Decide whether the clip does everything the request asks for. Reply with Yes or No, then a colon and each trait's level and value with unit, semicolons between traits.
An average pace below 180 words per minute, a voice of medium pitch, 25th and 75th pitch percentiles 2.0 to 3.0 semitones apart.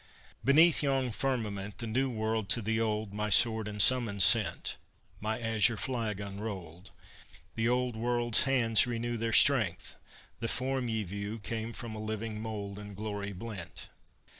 No: average, 155 wpm; low, 110 Hz; narrow, 2.5 semitones